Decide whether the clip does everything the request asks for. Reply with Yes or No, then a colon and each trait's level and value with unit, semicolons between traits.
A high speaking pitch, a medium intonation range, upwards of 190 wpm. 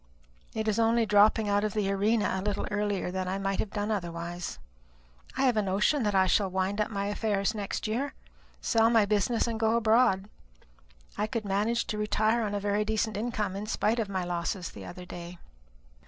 No: high, 210 Hz; narrow, 2.1 semitones; average, 200 wpm